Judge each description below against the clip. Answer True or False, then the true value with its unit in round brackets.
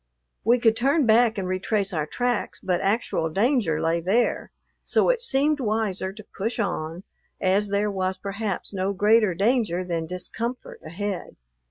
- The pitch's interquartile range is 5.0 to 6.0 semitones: False (3.9 semitones)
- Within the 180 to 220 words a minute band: False (155 wpm)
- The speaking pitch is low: False (200 Hz)